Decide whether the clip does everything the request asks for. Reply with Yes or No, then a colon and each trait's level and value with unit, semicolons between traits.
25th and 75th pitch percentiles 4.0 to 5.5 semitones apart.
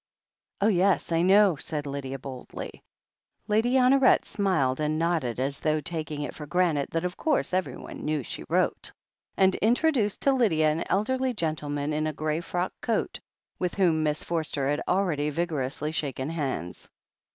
Yes: average, 4.7 semitones